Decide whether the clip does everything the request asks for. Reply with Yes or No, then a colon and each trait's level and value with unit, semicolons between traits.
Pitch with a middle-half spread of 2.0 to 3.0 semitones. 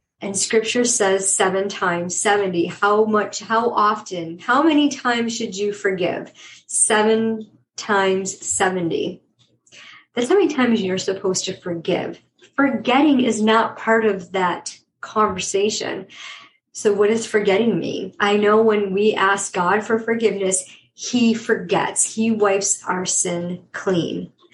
Yes: average, 2.7 semitones